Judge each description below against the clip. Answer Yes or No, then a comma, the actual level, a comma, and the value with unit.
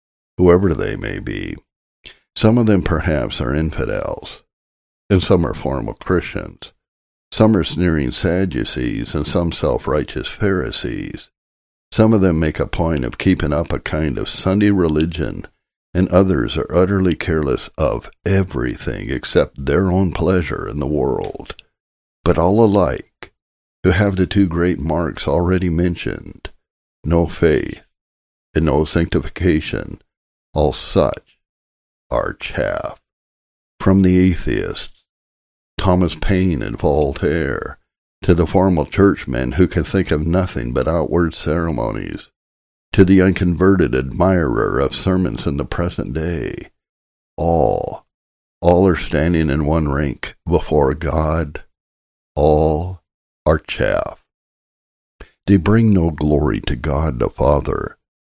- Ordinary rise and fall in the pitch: Yes, average, 4.7 semitones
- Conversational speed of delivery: No, slow, 125 wpm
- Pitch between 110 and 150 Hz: No, very low, 80 Hz